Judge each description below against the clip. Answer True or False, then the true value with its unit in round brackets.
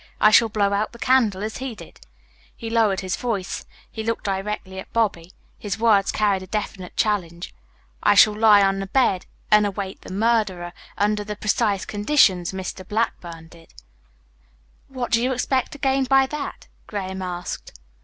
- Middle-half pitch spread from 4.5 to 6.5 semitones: False (3.2 semitones)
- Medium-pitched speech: False (210 Hz)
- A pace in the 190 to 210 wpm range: False (170 wpm)